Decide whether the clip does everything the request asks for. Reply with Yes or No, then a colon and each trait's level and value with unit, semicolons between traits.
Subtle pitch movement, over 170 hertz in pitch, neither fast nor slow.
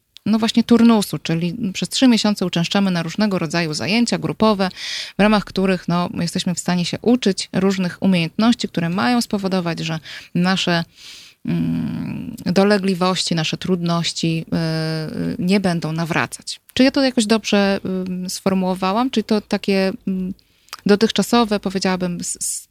No: average, 3.6 semitones; high, 190 Hz; average, 135 wpm